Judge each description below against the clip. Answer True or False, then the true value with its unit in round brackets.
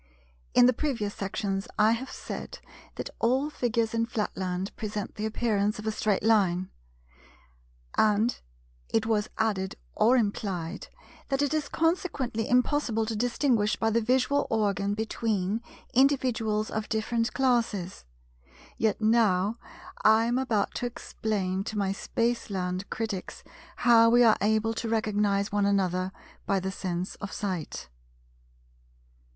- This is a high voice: True (220 Hz)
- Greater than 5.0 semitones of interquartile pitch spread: False (2.8 semitones)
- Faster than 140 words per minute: False (135 wpm)